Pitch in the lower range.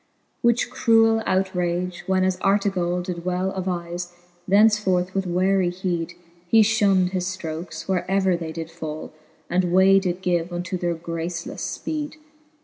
No: medium, 180 Hz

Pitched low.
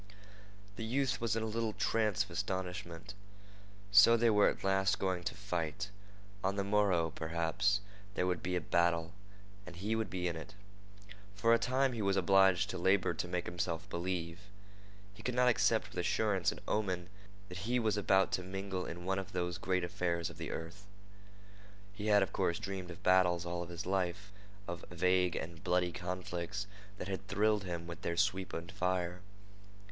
Yes: very low, 95 Hz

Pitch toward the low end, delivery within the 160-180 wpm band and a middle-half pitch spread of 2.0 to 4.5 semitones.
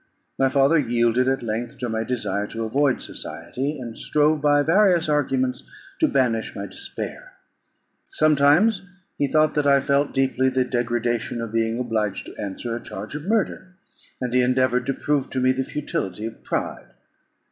Yes: low, 130 Hz; average, 170 wpm; average, 3.8 semitones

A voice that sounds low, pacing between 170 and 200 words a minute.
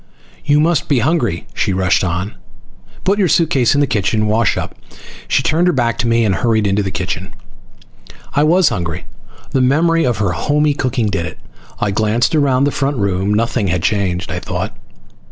Yes: low, 115 Hz; average, 190 wpm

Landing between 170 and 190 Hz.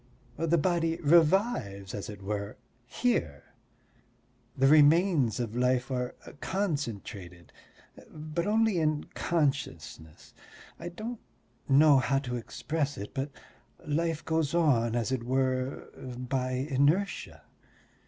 No: medium, 140 Hz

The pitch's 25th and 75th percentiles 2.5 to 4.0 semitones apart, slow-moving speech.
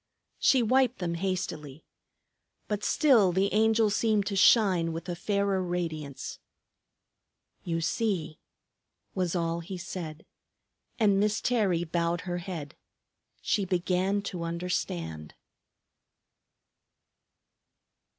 Yes: average, 3.3 semitones; slow, 100 wpm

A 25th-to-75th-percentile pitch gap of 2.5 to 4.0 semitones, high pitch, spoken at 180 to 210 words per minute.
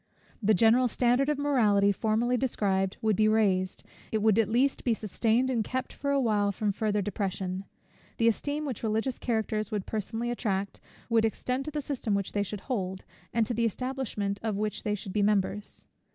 Yes: average, 3.2 semitones; high, 220 Hz; average, 190 wpm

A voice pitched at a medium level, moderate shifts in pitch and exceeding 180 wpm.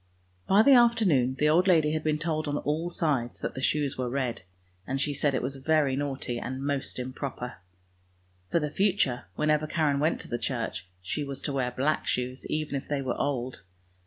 Yes: medium, 145 Hz; average, 3.0 semitones; average, 200 wpm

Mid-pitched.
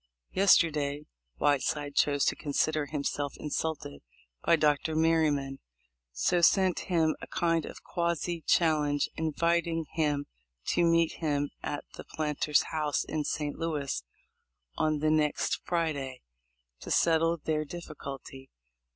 Yes: medium, 155 Hz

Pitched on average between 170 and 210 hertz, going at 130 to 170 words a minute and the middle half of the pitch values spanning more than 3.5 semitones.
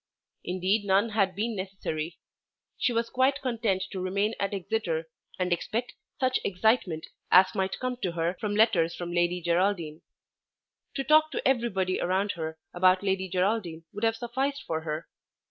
Yes: high, 190 Hz; average, 160 wpm; average, 4.3 semitones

